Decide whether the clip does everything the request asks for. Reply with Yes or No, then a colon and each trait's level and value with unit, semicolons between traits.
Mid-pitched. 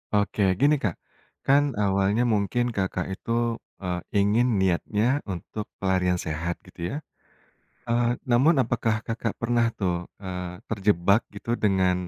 No: low, 100 Hz